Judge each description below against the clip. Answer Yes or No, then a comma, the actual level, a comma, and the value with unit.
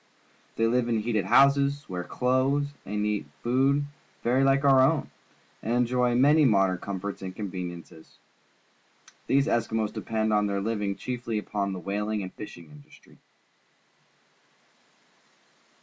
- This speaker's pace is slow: Yes, slow, 130 wpm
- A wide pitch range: No, average, 4.7 semitones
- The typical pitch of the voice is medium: No, low, 110 Hz